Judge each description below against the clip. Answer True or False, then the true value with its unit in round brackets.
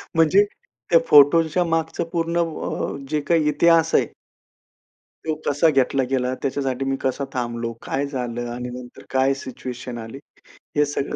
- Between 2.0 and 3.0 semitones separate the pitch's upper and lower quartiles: False (4.2 semitones)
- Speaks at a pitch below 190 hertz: True (135 Hz)